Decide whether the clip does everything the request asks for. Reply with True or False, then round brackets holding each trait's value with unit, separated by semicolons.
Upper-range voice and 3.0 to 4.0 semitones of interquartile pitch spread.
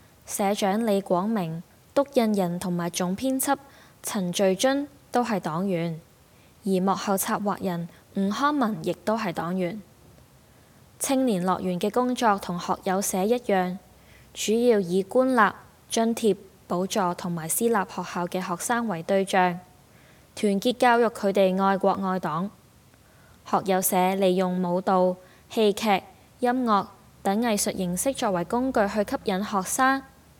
True (195 Hz; 3.5 semitones)